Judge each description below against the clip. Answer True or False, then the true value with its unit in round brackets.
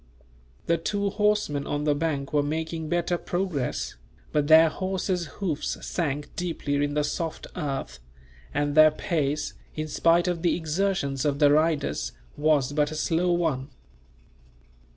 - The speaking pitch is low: False (155 Hz)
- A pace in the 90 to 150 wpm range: True (145 wpm)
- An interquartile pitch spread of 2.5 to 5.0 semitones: True (3.0 semitones)